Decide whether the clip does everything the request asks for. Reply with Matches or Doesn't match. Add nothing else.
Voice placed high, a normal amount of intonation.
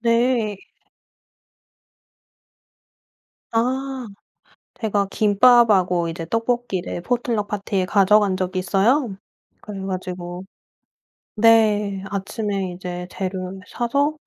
Matches